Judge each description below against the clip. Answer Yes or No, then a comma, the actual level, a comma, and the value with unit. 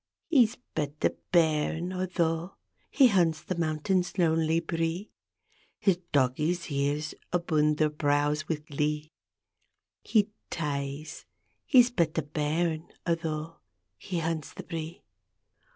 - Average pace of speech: No, slow, 115 wpm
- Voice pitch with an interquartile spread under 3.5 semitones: Yes, narrow, 2.5 semitones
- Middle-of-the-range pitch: Yes, medium, 160 Hz